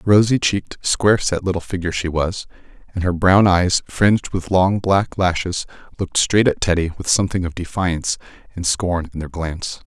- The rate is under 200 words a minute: Yes, average, 190 wpm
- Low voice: Yes, very low, 90 Hz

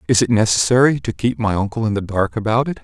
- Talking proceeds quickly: Yes, fast, 255 wpm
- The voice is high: No, low, 110 Hz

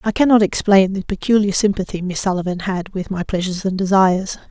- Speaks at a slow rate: No, average, 185 wpm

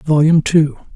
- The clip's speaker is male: Yes, male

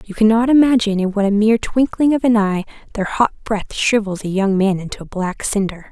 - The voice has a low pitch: No, high, 210 Hz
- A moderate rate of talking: No, fast, 225 wpm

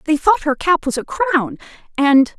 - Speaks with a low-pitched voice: No, very high, 305 Hz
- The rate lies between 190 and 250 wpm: Yes, average, 200 wpm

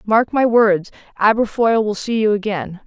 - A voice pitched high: Yes, high, 215 Hz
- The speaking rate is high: No, average, 165 wpm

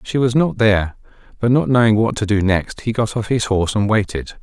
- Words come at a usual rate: No, fast, 245 wpm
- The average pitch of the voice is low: Yes, low, 110 Hz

